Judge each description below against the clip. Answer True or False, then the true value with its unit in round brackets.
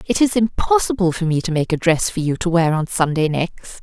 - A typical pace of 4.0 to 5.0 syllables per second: False (5.6 syllables/s)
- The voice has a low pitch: False (175 Hz)